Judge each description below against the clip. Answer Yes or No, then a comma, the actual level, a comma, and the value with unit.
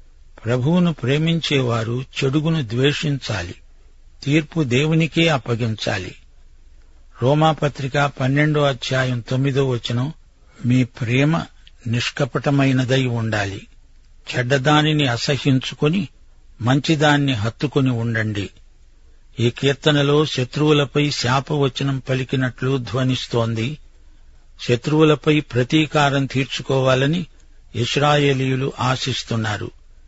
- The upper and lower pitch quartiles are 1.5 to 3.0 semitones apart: No, average, 3.8 semitones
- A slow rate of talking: Yes, slow, 65 wpm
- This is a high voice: No, low, 130 Hz